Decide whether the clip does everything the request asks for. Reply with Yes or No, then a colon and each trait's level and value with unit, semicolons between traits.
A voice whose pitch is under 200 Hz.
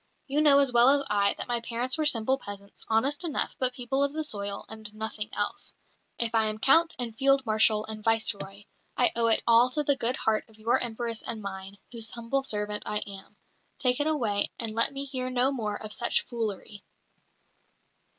No: high, 230 Hz